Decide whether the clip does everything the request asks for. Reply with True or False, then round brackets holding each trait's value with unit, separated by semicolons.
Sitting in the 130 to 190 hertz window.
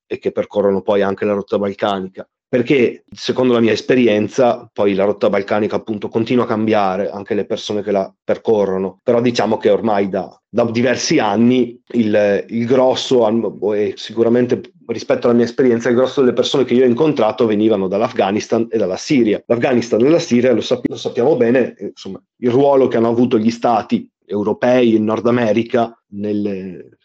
False (115 Hz)